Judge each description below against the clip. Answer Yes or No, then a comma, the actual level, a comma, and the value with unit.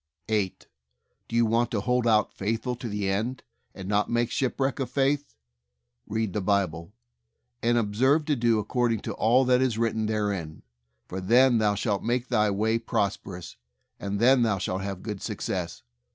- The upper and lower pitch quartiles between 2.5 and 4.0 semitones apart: Yes, average, 3.2 semitones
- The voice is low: Yes, low, 110 Hz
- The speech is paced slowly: No, average, 175 wpm